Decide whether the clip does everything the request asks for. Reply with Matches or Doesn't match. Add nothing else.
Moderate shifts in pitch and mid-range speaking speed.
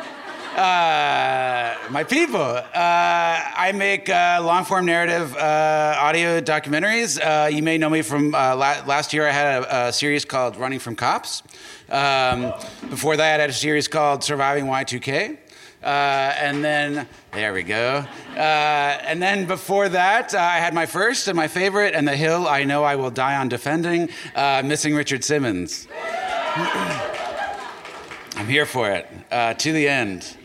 Matches